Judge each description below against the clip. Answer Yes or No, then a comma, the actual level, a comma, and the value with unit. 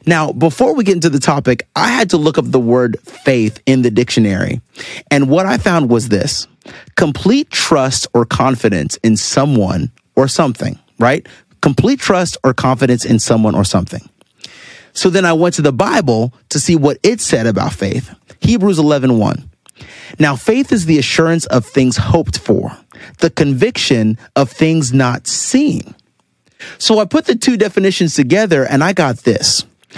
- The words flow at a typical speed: Yes, average, 165 wpm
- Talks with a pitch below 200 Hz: Yes, medium, 140 Hz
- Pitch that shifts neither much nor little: No, wide, 6.2 semitones